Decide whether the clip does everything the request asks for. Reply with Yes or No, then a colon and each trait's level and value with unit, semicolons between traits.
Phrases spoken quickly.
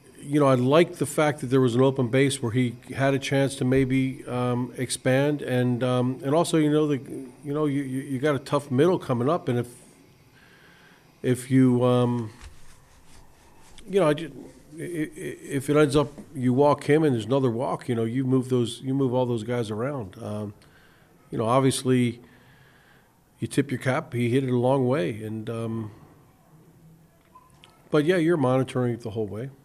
No: average, 190 wpm